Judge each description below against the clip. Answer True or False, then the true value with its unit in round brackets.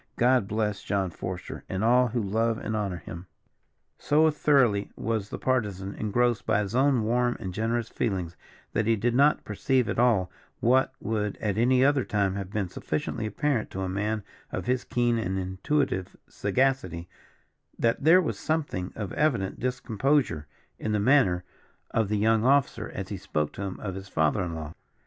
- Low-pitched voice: True (110 Hz)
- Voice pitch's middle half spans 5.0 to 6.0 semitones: False (4.6 semitones)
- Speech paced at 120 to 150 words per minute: False (175 wpm)